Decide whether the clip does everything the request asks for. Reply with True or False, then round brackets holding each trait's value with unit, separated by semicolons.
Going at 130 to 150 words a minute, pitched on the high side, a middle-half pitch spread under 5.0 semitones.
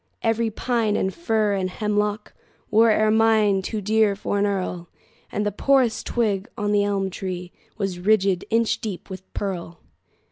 True (140 wpm; 205 Hz; 2.4 semitones)